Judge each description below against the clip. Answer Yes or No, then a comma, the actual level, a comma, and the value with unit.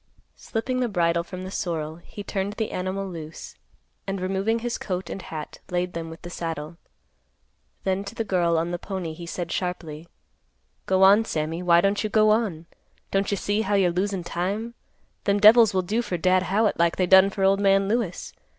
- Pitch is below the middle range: No, high, 190 Hz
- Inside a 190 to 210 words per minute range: Yes, average, 195 wpm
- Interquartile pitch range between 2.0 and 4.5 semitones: Yes, average, 2.9 semitones